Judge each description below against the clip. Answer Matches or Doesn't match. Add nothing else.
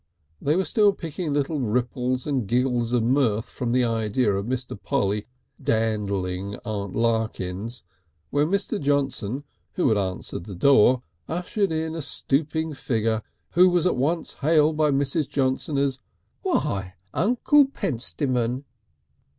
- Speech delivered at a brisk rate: Doesn't match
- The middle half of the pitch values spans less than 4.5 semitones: Doesn't match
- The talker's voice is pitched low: Matches